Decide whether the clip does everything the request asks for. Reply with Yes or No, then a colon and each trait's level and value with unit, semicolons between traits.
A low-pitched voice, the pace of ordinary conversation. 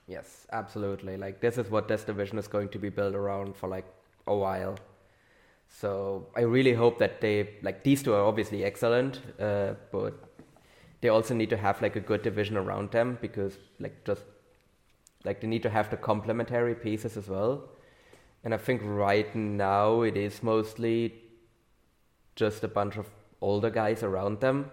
Yes: low, 105 Hz; average, 175 wpm